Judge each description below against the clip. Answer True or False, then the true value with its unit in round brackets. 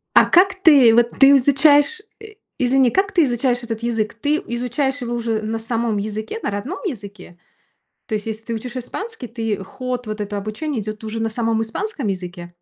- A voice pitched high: True (235 Hz)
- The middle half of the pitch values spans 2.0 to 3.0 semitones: False (4.1 semitones)